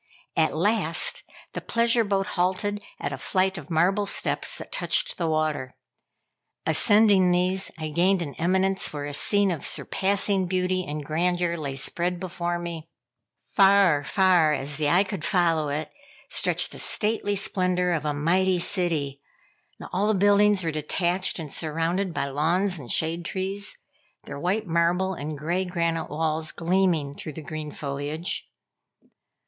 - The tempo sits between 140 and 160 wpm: Yes, average, 155 wpm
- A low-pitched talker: No, medium, 175 Hz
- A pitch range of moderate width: Yes, average, 3.5 semitones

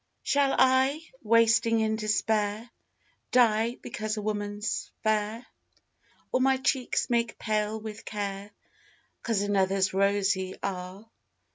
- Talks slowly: Yes, slow, 110 wpm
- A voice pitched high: Yes, high, 215 Hz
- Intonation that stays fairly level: Yes, narrow, 2.2 semitones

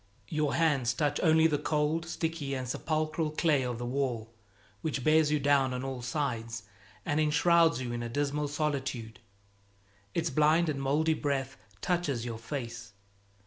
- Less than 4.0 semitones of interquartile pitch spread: Yes, average, 3.6 semitones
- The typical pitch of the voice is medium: Yes, medium, 145 Hz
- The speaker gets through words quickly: No, average, 155 wpm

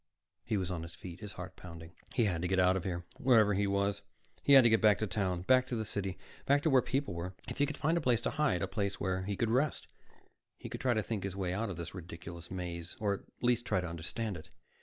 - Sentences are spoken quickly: Yes, fast, 270 wpm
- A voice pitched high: No, low, 100 Hz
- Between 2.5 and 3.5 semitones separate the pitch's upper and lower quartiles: No, average, 4.3 semitones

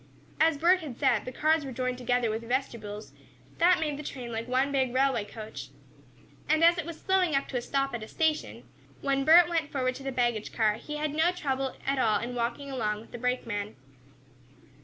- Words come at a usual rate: No, fast, 210 wpm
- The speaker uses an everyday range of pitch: Yes, average, 4.3 semitones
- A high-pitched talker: Yes, very high, 265 Hz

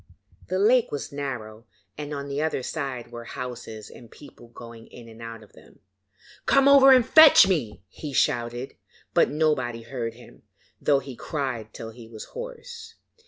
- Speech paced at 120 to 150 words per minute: No, average, 165 wpm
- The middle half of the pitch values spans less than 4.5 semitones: No, average, 5.2 semitones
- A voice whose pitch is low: Yes, low, 130 Hz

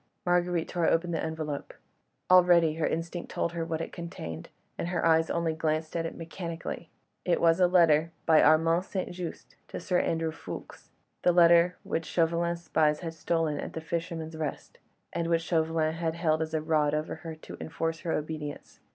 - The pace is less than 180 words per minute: No, average, 185 wpm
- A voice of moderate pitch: Yes, medium, 165 Hz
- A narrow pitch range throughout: Yes, narrow, 1.3 semitones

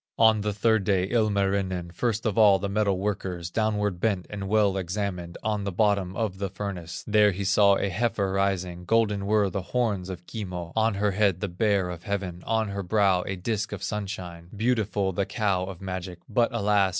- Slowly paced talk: No, average, 195 wpm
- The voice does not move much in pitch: Yes, narrow, 2.3 semitones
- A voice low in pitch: Yes, low, 100 Hz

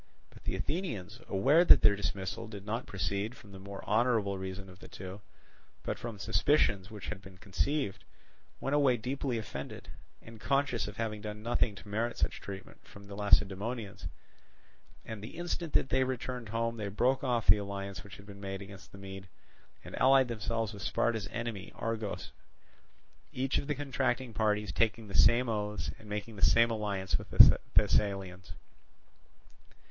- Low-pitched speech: Yes, low, 105 Hz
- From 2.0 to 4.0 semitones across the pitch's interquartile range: Yes, average, 3.2 semitones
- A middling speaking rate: Yes, average, 170 wpm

